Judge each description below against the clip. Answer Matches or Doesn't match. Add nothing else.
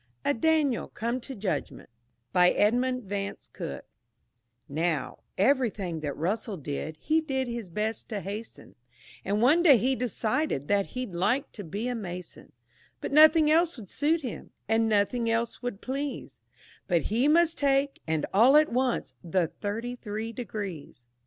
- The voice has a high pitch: Matches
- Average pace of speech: Matches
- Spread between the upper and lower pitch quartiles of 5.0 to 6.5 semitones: Matches